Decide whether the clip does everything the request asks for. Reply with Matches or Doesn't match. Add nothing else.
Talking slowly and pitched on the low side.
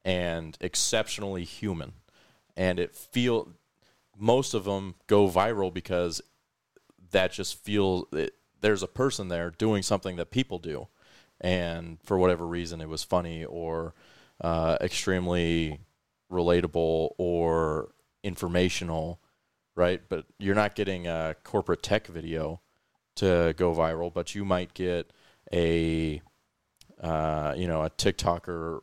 Matches